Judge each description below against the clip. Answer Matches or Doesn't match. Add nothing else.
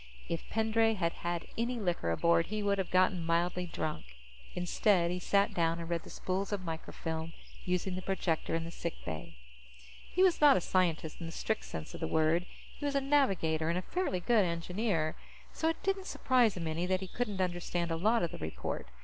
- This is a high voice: Doesn't match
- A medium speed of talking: Doesn't match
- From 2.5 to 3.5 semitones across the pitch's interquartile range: Doesn't match